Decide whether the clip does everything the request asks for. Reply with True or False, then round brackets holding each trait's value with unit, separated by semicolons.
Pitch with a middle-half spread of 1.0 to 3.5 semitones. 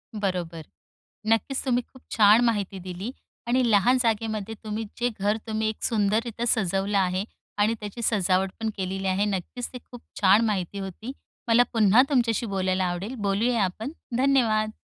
True (3.1 semitones)